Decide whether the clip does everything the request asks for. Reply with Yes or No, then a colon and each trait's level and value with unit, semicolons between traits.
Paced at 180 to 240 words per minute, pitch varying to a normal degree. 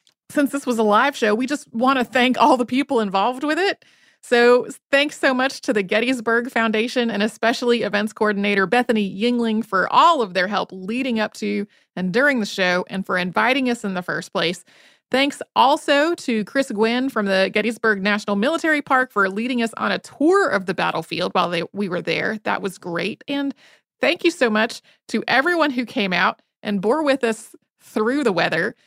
Yes: average, 200 wpm; average, 4.6 semitones